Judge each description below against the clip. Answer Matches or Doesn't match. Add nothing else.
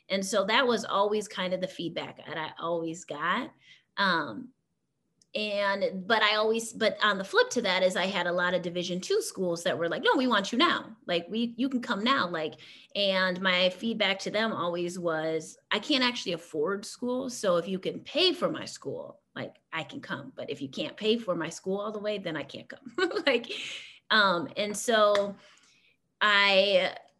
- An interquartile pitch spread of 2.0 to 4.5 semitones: Doesn't match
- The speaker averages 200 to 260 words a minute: Matches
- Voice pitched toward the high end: Matches